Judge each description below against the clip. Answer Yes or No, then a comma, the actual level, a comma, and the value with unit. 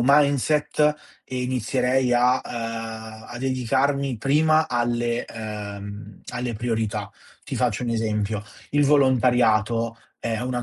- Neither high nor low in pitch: No, low, 120 Hz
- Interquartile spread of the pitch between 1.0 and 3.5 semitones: Yes, average, 2.8 semitones